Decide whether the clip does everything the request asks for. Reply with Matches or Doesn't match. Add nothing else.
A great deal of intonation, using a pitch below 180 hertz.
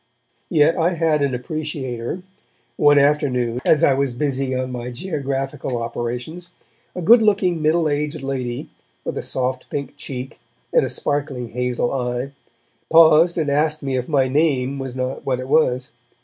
Doesn't match